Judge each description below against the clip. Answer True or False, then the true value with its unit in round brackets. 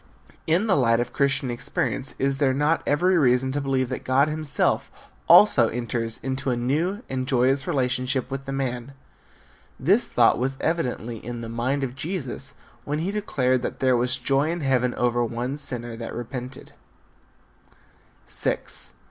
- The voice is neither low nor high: False (130 Hz)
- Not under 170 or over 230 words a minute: False (155 wpm)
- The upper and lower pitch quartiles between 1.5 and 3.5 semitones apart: True (2.5 semitones)